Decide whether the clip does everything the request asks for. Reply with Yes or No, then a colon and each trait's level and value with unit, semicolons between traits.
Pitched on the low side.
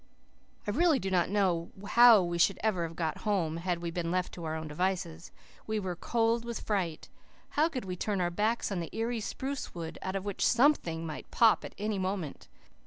No: high, 190 Hz